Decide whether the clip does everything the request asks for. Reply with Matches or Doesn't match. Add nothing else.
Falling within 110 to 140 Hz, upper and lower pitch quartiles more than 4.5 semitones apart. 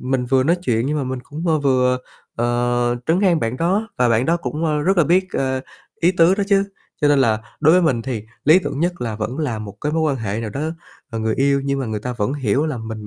Matches